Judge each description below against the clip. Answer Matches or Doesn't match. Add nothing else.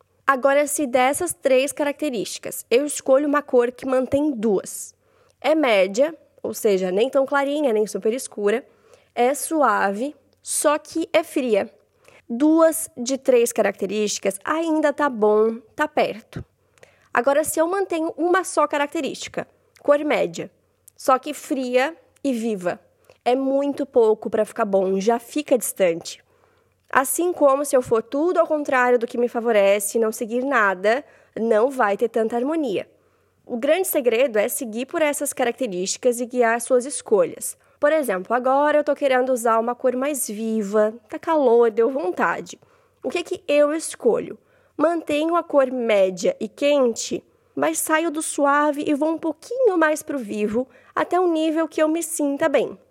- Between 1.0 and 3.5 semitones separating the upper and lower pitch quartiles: Doesn't match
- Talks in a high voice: Matches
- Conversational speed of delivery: Matches